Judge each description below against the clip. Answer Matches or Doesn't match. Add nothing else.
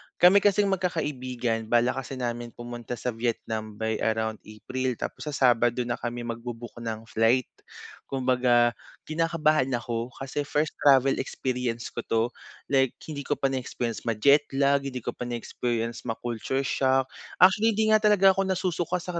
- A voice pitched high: Doesn't match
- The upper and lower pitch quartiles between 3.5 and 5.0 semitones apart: Matches